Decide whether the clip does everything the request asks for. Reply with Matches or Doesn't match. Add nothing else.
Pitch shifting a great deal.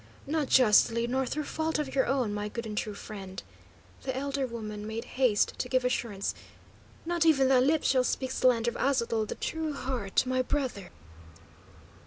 Doesn't match